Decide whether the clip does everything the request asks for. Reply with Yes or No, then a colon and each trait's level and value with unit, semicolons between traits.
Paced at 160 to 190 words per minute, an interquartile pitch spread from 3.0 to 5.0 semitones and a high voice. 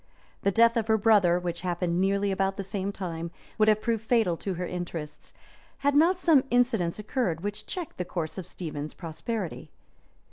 Yes: average, 180 wpm; average, 4.4 semitones; high, 195 Hz